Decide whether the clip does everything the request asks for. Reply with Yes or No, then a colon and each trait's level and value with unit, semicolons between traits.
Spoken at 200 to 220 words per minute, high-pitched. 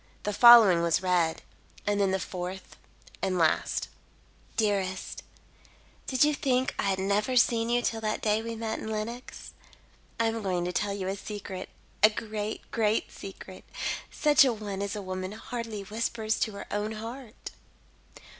No: average, 165 wpm; high, 210 Hz